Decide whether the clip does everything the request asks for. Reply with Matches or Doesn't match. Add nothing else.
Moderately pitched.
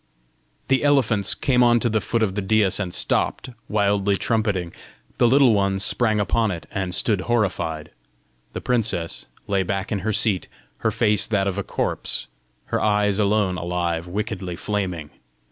Doesn't match